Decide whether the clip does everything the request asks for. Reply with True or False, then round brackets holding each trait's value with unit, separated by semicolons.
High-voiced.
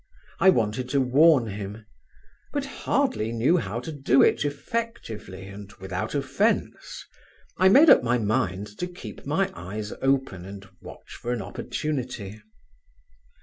False (115 Hz)